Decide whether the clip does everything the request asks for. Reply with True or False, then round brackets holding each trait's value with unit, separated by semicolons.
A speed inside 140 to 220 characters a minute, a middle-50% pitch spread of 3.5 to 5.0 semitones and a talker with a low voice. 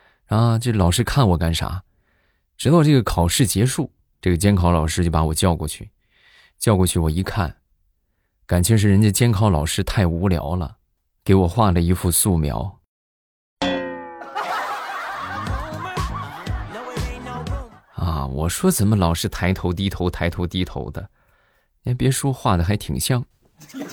True (200 characters per minute; 4.1 semitones; 90 Hz)